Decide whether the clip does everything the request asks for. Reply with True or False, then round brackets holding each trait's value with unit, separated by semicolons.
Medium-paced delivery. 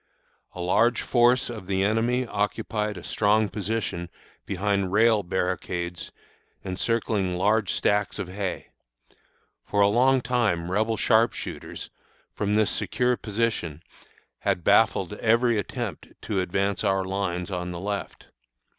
False (130 wpm)